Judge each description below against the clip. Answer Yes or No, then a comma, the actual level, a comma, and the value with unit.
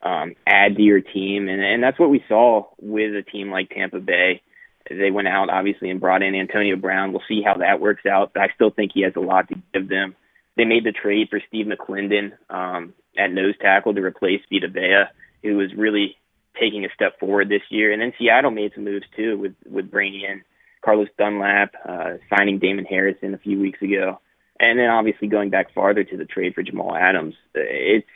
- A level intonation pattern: Yes, narrow, 1.4 semitones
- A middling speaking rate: No, fast, 215 wpm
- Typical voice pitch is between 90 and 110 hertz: Yes, low, 100 Hz